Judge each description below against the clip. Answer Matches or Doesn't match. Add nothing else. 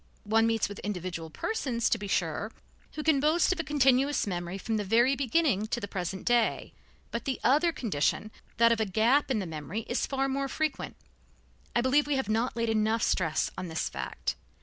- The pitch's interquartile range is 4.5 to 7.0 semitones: Matches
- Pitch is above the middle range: Matches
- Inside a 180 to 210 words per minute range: Matches